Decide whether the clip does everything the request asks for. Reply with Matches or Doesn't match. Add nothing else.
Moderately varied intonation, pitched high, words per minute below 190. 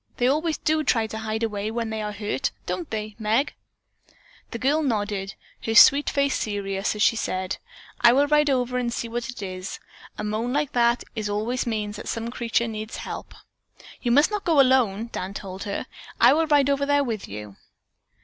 Doesn't match